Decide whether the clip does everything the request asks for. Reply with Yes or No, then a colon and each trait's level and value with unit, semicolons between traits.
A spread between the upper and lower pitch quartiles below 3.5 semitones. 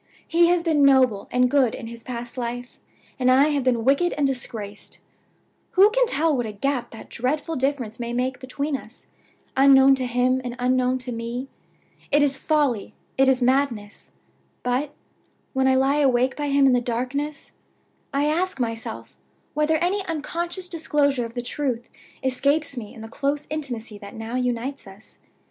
Yes: average, 3.0 semitones